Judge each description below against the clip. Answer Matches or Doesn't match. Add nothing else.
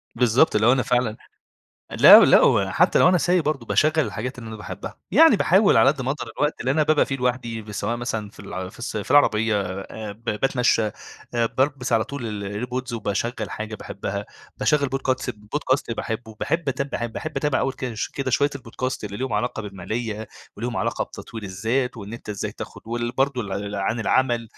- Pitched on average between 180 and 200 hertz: Doesn't match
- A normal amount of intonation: Matches